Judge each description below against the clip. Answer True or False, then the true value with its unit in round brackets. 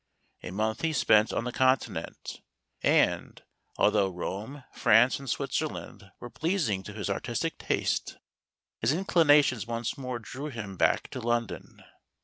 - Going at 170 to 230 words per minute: False (135 wpm)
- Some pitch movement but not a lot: True (4.4 semitones)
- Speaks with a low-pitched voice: True (120 Hz)